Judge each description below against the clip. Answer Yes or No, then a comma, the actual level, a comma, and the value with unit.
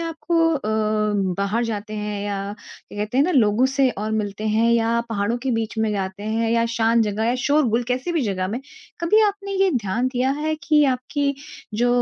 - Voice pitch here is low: No, high, 230 Hz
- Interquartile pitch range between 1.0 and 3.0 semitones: No, average, 4.4 semitones